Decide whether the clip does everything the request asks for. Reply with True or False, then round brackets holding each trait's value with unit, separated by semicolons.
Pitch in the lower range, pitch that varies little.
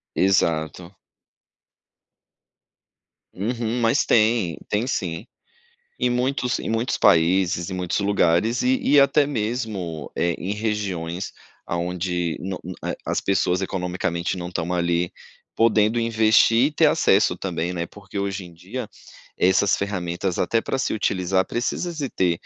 False (95 Hz; 4.5 semitones)